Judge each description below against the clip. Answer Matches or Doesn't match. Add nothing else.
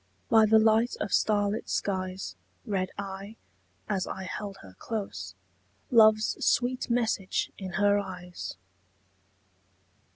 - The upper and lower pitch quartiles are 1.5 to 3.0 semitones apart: Matches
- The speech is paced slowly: Matches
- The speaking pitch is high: Matches